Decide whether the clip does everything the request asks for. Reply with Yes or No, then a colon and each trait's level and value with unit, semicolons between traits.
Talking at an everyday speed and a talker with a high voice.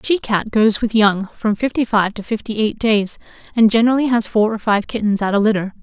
No: fast, 235 wpm; high, 220 Hz